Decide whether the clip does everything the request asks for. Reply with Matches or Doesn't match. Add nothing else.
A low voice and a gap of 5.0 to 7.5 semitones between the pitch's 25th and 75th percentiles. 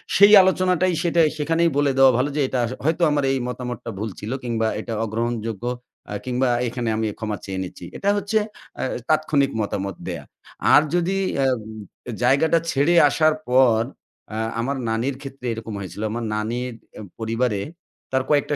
Matches